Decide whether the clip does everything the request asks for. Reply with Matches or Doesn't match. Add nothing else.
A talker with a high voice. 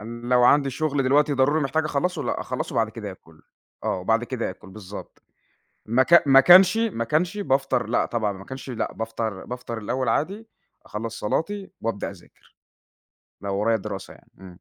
Doesn't match